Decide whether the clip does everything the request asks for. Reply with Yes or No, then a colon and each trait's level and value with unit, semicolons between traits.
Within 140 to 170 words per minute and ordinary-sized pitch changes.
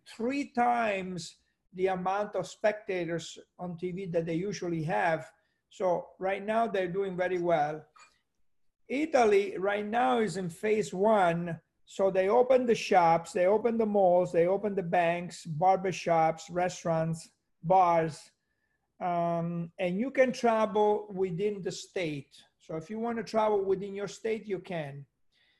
Yes: average, 145 wpm; average, 3.8 semitones